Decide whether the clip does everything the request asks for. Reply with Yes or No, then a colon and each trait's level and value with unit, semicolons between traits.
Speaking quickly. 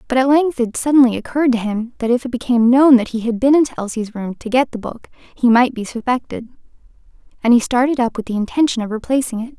Yes: fast, 240 wpm